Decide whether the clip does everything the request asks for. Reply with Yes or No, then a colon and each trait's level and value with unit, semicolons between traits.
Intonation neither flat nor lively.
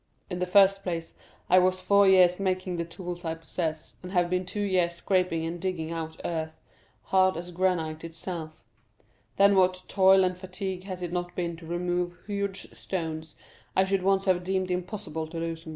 No: narrow, 2.1 semitones